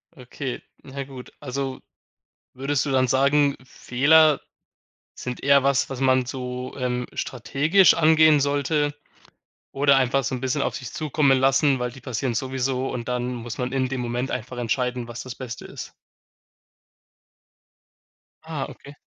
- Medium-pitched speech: No, low, 130 Hz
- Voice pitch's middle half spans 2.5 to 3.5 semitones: No, narrow, 1.9 semitones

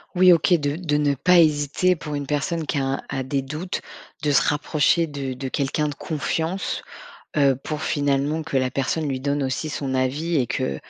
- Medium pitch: Yes, medium, 145 Hz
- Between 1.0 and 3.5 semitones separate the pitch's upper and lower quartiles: Yes, narrow, 2.6 semitones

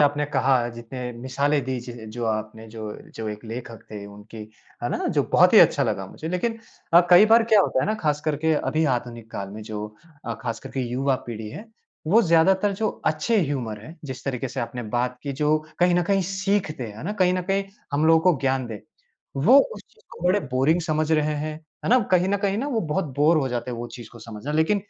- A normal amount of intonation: No, wide, 6.8 semitones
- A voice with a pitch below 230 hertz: Yes, medium, 140 Hz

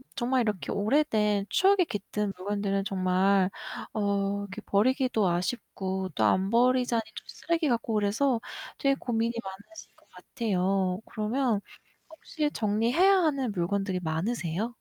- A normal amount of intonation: Yes, average, 4.3 semitones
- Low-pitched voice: No, high, 210 Hz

